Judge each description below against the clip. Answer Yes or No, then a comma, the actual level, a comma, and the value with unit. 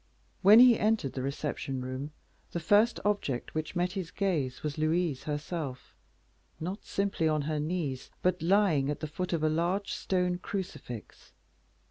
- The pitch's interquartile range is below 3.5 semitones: No, average, 4.3 semitones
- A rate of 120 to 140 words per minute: No, average, 155 wpm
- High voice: No, medium, 165 Hz